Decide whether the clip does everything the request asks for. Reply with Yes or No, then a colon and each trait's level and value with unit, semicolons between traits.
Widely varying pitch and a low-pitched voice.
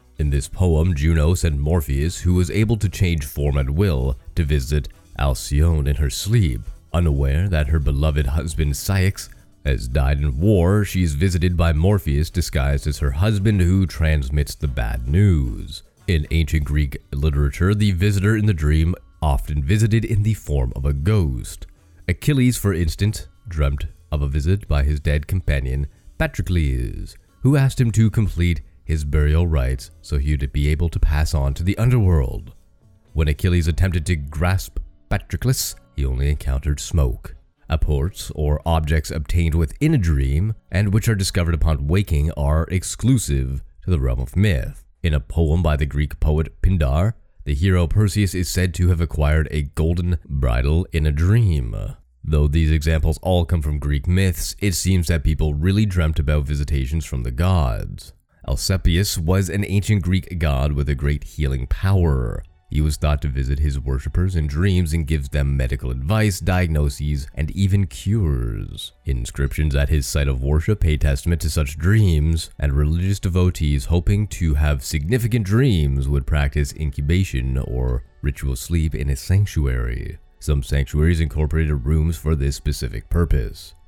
No: average, 4.0 semitones; very low, 80 Hz